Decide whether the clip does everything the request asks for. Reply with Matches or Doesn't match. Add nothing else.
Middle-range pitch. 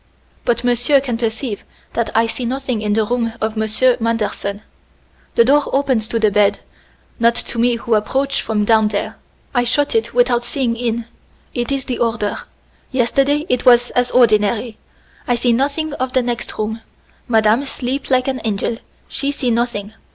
Doesn't match